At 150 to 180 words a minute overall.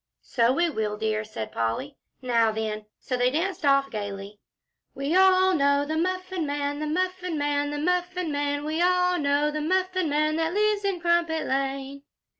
Yes: average, 175 wpm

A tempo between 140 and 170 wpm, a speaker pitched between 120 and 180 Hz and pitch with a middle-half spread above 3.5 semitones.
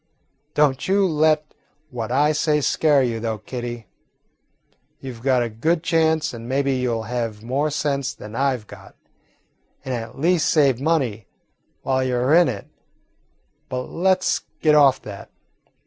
Yes: average, 165 wpm; low, 135 Hz; average, 4.3 semitones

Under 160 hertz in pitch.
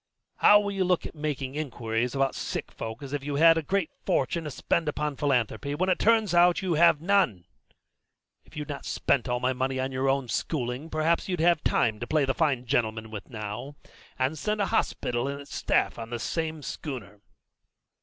Yes: medium, 140 Hz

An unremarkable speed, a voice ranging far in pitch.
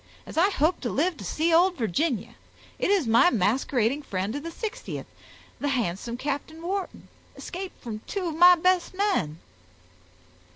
Yes: average, 160 wpm; wide, 7.3 semitones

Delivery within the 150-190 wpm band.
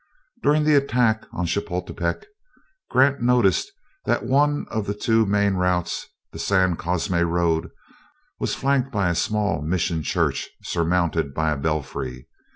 No: average, 140 wpm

